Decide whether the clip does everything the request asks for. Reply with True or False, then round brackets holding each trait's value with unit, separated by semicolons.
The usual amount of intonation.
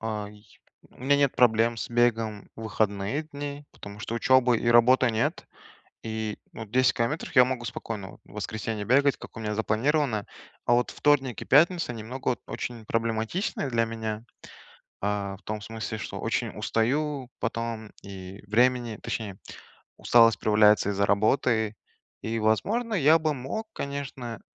True (3.3 semitones)